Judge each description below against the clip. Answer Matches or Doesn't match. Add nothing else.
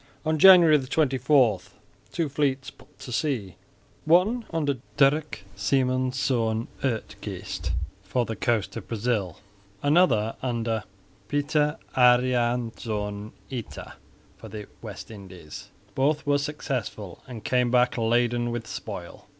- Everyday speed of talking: Doesn't match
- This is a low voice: Matches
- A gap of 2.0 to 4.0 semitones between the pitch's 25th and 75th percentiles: Doesn't match